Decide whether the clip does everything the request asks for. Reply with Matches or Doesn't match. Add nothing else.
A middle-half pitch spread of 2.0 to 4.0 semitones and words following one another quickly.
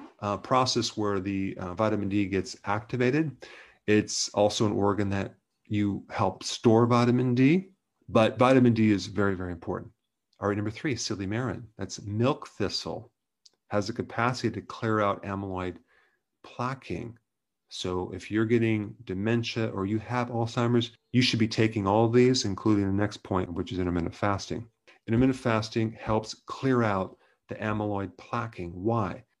Doesn't match